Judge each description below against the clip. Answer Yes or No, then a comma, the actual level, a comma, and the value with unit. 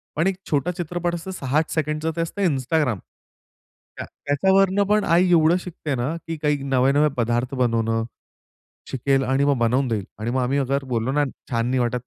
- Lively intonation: No, average, 4.7 semitones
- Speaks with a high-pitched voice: No, medium, 140 Hz